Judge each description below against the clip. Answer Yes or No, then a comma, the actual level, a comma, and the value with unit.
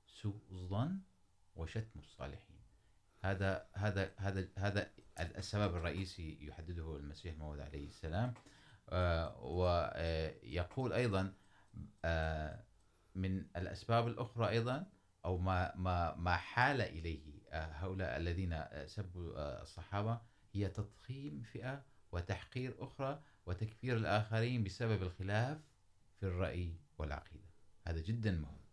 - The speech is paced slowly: Yes, slow, 95 wpm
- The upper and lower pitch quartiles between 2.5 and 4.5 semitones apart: Yes, average, 3.9 semitones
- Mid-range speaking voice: No, very low, 95 Hz